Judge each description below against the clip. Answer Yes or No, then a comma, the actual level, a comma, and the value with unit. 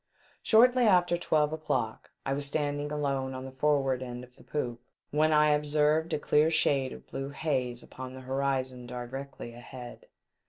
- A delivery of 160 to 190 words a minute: Yes, average, 170 wpm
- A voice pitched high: No, medium, 140 Hz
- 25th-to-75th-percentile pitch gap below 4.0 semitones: Yes, average, 2.8 semitones